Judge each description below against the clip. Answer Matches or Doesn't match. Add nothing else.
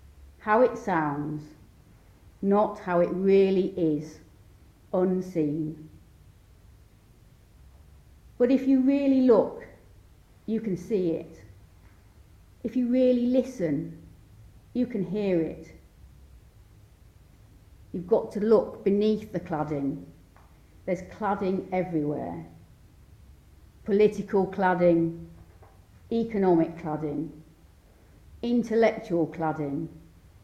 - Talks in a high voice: Doesn't match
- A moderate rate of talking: Doesn't match